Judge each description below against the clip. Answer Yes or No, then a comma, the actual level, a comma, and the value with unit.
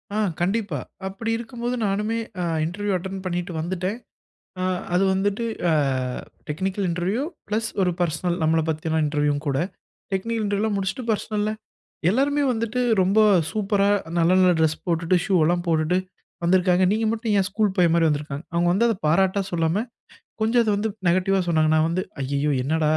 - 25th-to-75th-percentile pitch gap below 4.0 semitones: No, average, 4.3 semitones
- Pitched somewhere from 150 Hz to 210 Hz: Yes, high, 190 Hz